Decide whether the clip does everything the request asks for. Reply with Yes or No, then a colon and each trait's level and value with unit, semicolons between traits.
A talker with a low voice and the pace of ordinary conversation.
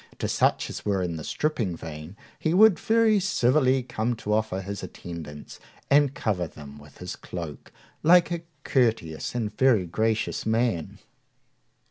Yes: low, 110 Hz; average, 150 wpm